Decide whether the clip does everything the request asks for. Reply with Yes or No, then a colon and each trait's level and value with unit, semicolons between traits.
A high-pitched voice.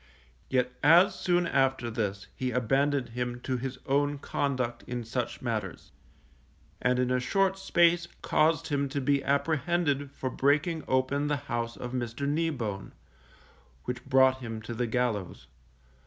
No: low, 130 Hz